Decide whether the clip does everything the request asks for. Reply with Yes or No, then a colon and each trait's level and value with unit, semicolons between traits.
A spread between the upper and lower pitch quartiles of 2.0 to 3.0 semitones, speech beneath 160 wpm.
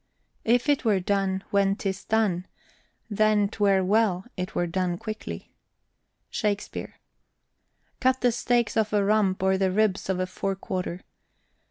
Yes: narrow, 2.4 semitones; average, 145 wpm